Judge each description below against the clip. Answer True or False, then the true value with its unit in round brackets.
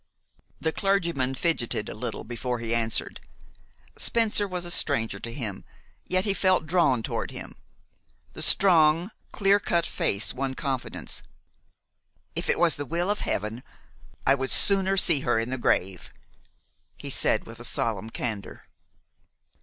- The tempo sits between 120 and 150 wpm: True (145 wpm)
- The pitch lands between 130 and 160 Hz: True (140 Hz)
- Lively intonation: True (7.5 semitones)